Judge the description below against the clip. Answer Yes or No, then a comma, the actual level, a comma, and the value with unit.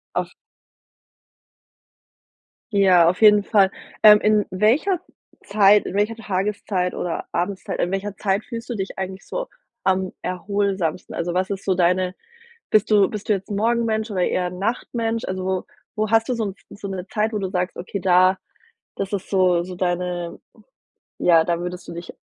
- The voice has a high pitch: Yes, high, 195 Hz